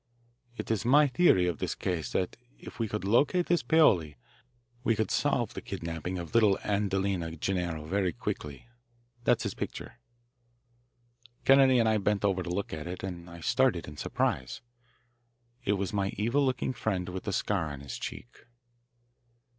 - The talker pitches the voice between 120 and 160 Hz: No, very low, 95 Hz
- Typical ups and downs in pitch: Yes, average, 5.0 semitones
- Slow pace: No, average, 165 wpm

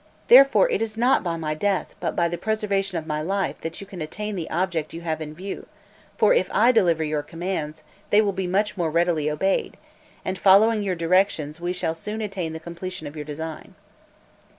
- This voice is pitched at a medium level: Yes, medium, 175 Hz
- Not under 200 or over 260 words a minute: Yes, fast, 205 wpm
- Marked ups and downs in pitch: No, average, 3.9 semitones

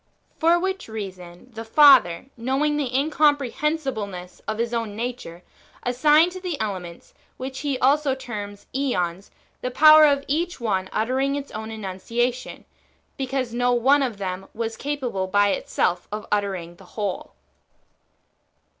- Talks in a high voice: Yes, high, 240 Hz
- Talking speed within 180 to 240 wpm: No, average, 140 wpm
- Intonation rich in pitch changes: Yes, wide, 5.7 semitones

